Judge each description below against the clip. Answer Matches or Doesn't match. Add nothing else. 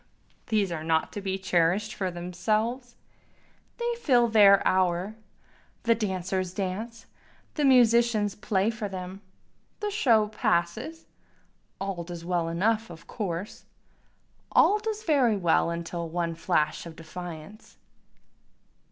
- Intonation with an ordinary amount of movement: Matches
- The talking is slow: Matches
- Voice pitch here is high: Matches